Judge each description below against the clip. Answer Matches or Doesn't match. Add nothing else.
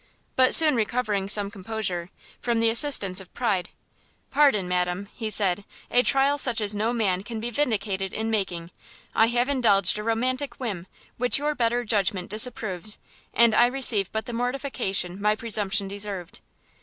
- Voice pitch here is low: Doesn't match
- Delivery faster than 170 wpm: Doesn't match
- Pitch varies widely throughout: Doesn't match